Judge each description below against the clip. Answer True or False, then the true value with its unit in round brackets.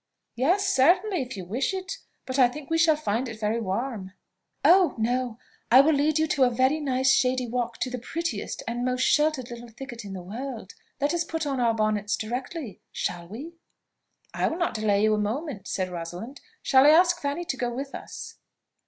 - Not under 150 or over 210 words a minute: True (200 wpm)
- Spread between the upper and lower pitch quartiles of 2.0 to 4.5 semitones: False (5.2 semitones)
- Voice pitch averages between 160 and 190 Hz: False (255 Hz)